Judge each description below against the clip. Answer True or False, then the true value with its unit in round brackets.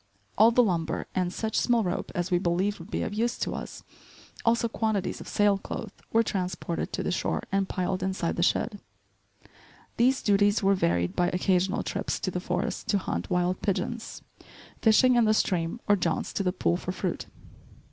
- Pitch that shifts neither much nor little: True (3.4 semitones)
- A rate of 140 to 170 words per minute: False (185 wpm)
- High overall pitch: True (195 Hz)